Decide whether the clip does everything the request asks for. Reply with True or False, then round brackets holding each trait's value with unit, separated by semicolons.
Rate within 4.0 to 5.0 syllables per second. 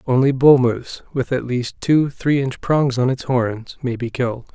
True (4.5 syllables/s)